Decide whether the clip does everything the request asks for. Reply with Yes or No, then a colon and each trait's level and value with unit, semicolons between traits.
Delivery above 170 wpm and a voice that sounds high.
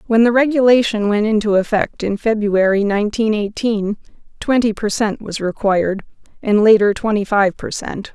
No: average, 155 wpm; high, 215 Hz